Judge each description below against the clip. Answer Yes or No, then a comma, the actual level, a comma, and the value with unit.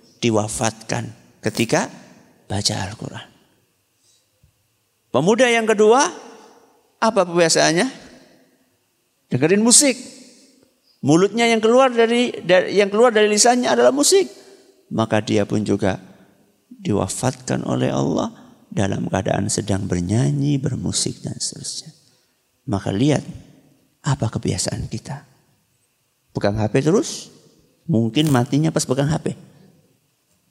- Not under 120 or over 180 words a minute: No, average, 95 wpm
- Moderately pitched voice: No, low, 130 Hz